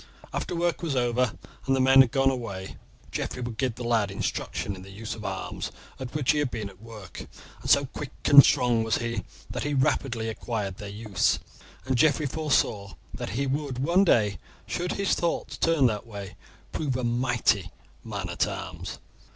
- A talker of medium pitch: No, low, 120 Hz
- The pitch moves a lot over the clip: No, average, 4.5 semitones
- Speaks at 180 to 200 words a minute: Yes, average, 190 wpm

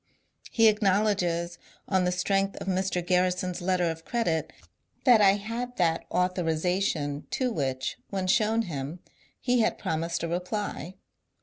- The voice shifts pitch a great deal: No, average, 3.4 semitones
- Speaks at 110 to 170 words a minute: Yes, slow, 135 wpm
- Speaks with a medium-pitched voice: Yes, medium, 180 Hz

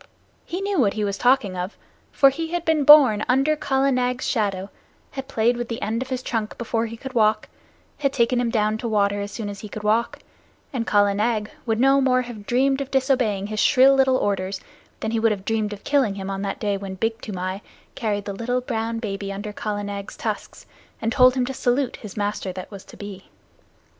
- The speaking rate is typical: No, fast, 220 wpm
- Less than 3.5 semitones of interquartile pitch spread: No, average, 4.0 semitones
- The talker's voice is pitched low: No, high, 225 Hz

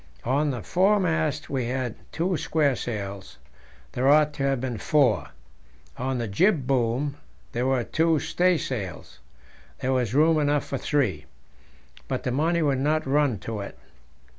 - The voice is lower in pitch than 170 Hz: Yes, low, 135 Hz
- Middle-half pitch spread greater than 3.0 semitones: Yes, average, 4.0 semitones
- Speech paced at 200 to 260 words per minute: No, average, 145 wpm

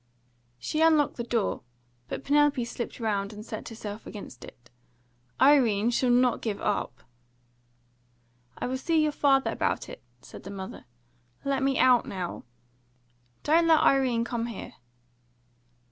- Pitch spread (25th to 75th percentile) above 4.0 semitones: Yes, average, 5.3 semitones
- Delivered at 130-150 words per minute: Yes, average, 145 wpm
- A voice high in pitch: Yes, high, 235 Hz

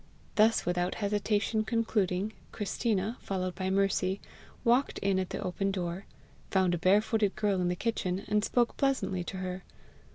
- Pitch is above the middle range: Yes, high, 195 Hz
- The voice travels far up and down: No, average, 2.8 semitones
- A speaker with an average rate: Yes, average, 155 wpm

